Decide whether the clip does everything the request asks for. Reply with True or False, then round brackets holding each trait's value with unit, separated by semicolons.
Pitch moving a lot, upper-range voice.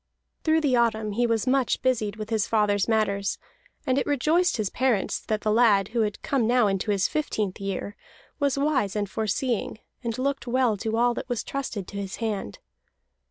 False (3.9 semitones; 225 Hz)